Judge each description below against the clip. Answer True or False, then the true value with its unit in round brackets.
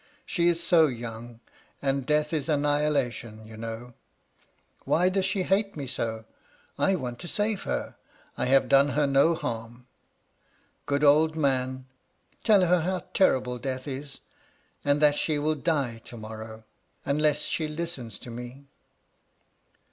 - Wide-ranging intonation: False (4.6 semitones)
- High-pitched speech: False (140 Hz)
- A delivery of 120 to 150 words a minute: True (145 wpm)